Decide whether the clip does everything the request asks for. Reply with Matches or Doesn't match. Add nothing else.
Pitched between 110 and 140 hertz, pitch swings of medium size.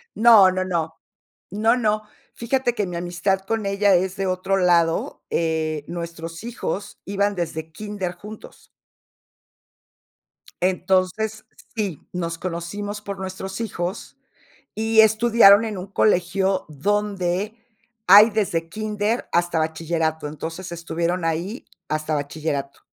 Doesn't match